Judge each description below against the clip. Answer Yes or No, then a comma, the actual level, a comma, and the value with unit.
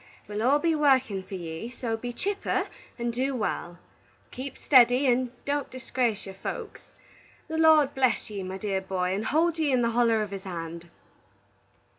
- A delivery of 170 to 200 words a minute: Yes, average, 175 wpm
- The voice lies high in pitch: Yes, high, 240 Hz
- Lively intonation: Yes, wide, 5.8 semitones